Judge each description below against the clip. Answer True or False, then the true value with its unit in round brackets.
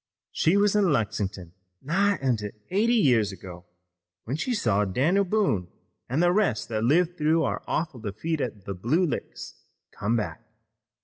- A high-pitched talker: False (135 Hz)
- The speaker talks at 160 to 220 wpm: True (165 wpm)